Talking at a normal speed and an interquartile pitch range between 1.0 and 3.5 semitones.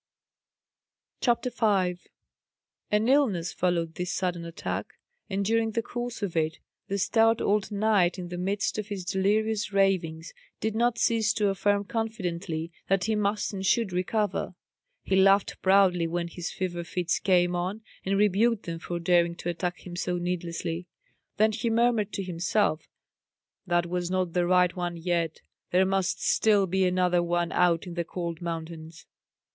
Yes: average, 160 wpm; average, 3.1 semitones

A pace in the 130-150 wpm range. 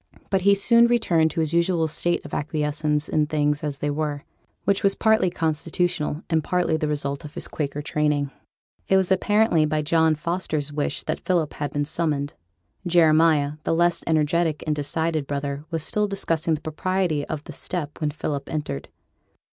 No: average, 175 wpm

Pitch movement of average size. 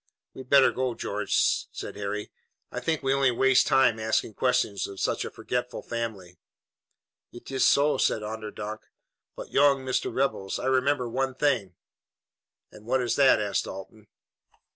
Yes: average, 4.0 semitones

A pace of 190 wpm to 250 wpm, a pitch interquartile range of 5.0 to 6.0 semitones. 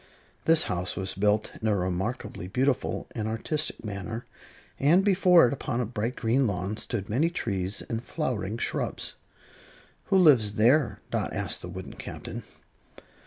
No: average, 150 wpm; wide, 5.6 semitones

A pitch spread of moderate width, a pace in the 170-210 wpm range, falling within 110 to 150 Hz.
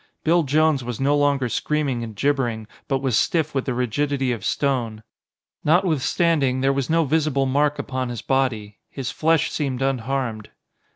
No: average, 3.1 semitones; average, 160 wpm; low, 135 Hz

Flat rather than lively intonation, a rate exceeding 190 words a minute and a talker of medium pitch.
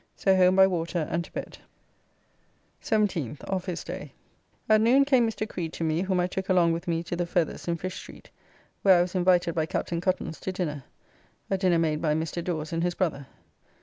Yes: narrow, 2.3 semitones; fast, 205 wpm; medium, 175 Hz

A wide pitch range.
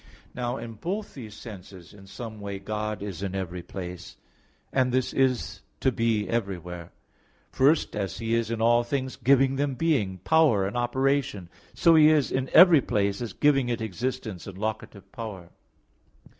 No: average, 5.0 semitones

